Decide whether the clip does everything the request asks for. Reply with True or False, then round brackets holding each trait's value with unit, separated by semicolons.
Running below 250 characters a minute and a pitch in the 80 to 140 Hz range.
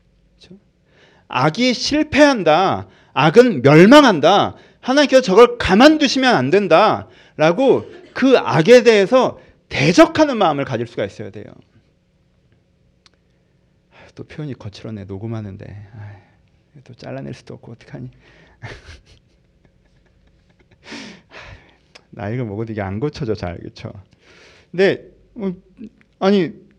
False (215 characters per minute; 170 Hz)